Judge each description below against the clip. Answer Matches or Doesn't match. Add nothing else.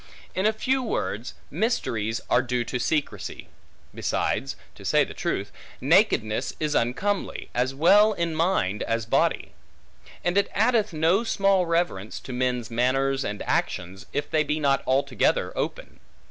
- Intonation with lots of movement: Matches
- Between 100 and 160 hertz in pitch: Matches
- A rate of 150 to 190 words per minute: Doesn't match